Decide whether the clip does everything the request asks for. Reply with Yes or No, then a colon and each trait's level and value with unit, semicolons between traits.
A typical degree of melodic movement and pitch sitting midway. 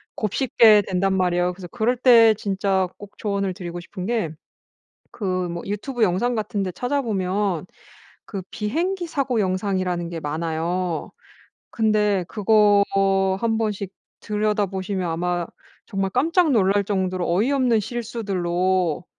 No: average, 3.4 semitones; high, 200 Hz